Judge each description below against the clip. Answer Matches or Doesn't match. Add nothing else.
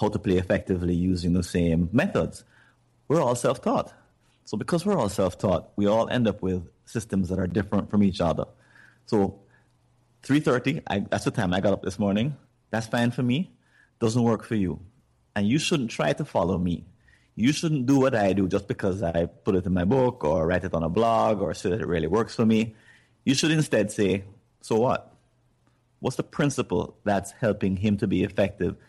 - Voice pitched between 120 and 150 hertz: Doesn't match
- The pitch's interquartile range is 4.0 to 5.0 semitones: Matches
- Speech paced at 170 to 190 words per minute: Doesn't match